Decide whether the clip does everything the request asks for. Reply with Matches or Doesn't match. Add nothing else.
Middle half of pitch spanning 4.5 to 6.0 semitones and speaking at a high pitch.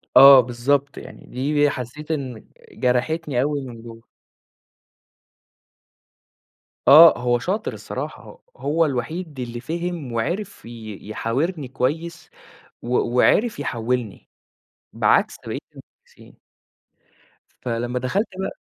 Doesn't match